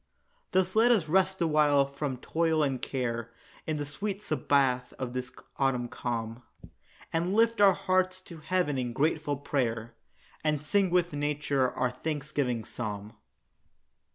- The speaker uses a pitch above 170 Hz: No, medium, 145 Hz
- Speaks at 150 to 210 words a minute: No, average, 140 wpm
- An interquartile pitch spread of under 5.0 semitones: No, wide, 5.5 semitones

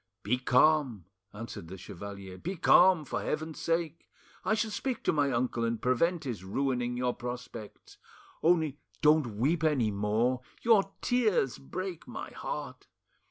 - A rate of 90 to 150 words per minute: Yes, average, 145 wpm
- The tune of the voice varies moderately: No, wide, 6.2 semitones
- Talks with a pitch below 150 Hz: Yes, low, 135 Hz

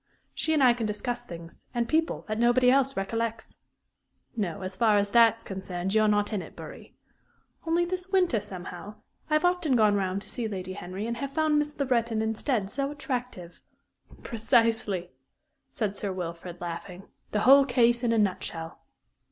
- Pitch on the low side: No, high, 225 Hz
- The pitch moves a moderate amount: Yes, average, 4.7 semitones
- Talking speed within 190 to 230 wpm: No, average, 175 wpm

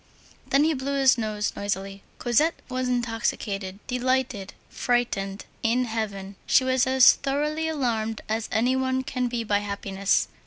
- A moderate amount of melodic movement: Yes, average, 4.0 semitones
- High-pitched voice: Yes, high, 240 Hz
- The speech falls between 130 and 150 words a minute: Yes, average, 145 wpm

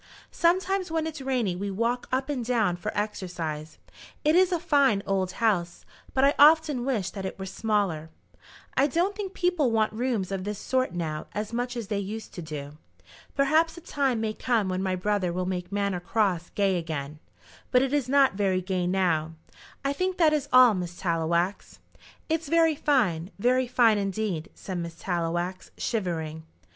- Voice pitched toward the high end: Yes, high, 210 Hz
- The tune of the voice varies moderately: No, wide, 6.9 semitones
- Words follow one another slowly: No, average, 180 wpm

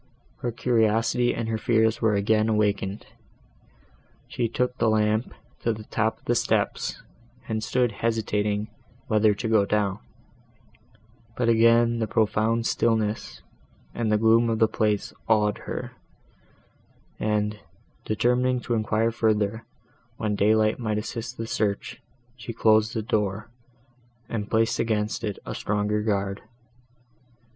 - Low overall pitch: Yes, low, 110 Hz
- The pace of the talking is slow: Yes, slow, 130 wpm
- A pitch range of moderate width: No, narrow, 1.6 semitones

